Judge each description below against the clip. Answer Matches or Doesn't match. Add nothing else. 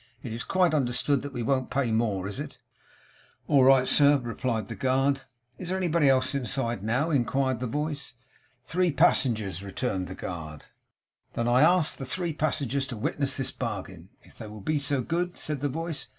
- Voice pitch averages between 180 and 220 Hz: Doesn't match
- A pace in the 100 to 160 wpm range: Doesn't match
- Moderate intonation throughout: Matches